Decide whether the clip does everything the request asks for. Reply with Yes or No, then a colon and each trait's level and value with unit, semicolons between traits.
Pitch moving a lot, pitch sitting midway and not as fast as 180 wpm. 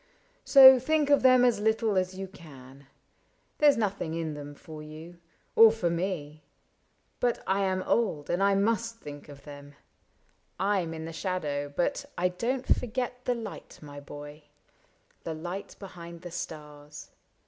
Yes: wide, 6.8 semitones; medium, 180 Hz; average, 170 wpm